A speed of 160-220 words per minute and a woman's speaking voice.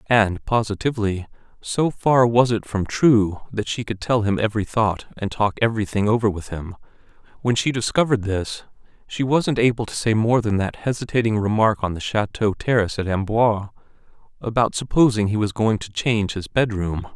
No: average, 175 wpm; male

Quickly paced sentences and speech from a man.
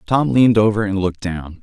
Yes: fast, 220 wpm; male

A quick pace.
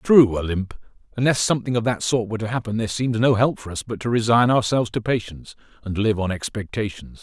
Yes: fast, 215 wpm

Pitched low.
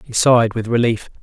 Yes: low, 115 Hz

